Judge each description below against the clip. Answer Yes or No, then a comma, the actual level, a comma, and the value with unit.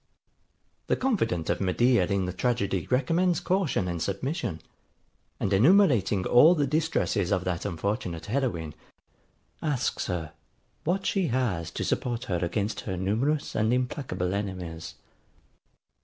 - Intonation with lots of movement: Yes, wide, 7.3 semitones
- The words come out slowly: Yes, slow, 125 wpm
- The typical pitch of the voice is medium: No, low, 105 Hz